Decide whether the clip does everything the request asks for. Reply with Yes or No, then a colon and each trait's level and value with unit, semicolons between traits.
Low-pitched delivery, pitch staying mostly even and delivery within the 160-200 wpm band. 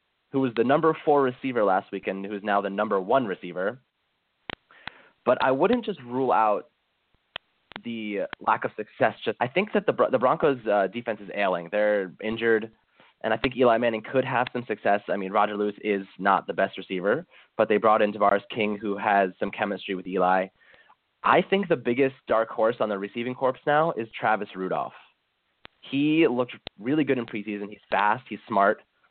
No: low, 110 Hz; average, 3.8 semitones; average, 185 wpm